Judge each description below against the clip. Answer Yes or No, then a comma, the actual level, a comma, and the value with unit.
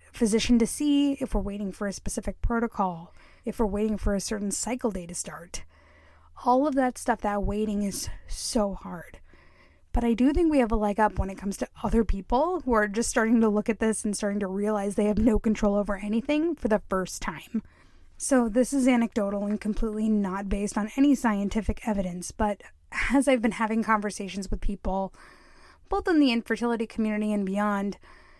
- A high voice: Yes, high, 215 Hz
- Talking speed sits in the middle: Yes, average, 195 wpm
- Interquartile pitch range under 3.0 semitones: Yes, narrow, 2.6 semitones